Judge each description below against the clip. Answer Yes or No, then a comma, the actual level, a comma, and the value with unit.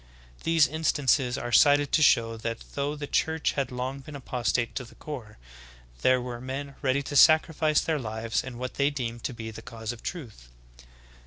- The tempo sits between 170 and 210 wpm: Yes, average, 185 wpm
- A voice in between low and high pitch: No, low, 130 Hz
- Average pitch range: Yes, average, 3.6 semitones